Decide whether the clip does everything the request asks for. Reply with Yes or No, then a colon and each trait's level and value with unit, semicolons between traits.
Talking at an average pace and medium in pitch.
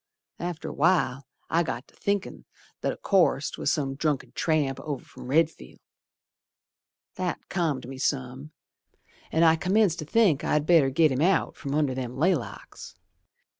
Yes: average, 155 wpm; medium, 155 Hz